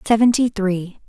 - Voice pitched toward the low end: No, high, 210 Hz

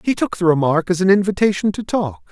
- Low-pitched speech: No, medium, 180 Hz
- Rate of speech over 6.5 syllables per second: No, 6.0 syllables/s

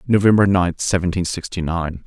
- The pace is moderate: Yes, average, 145 wpm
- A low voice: Yes, very low, 90 Hz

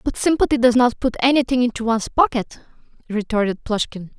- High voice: Yes, high, 240 Hz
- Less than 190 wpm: Yes, average, 160 wpm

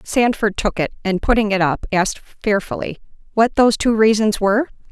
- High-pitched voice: Yes, high, 210 Hz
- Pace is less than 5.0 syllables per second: No, 5.6 syllables/s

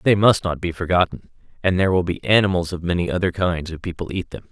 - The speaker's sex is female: No, male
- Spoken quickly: Yes, fast, 240 wpm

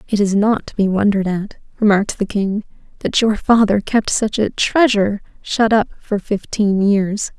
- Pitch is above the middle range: Yes, high, 205 Hz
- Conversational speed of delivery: Yes, average, 180 wpm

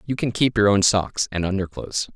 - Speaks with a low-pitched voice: Yes, low, 100 Hz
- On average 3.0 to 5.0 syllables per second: No, 5.6 syllables/s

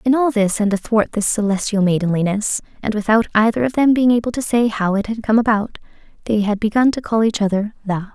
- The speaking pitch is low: No, high, 215 Hz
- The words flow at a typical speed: No, fast, 220 wpm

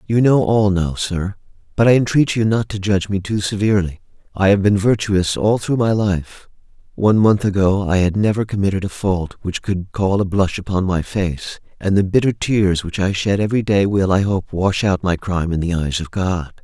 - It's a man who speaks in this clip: Yes, male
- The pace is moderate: No, fast, 220 wpm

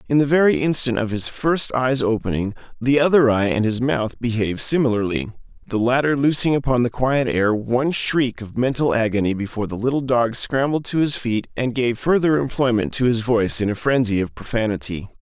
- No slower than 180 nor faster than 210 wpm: Yes, average, 195 wpm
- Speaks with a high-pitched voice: No, low, 120 Hz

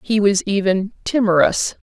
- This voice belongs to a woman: Yes, female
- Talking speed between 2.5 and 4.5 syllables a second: Yes, 4.4 syllables/s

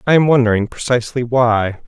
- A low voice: Yes, low, 120 Hz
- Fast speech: No, average, 160 wpm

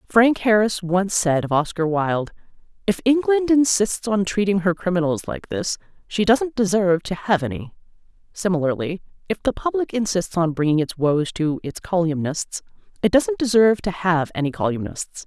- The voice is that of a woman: Yes, female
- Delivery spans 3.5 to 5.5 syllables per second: Yes, 5.0 syllables/s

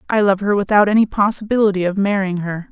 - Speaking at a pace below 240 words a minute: Yes, average, 200 wpm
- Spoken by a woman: Yes, female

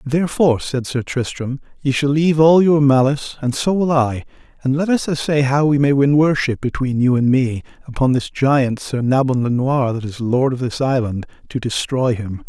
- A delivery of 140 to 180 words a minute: No, fast, 205 wpm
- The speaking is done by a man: Yes, male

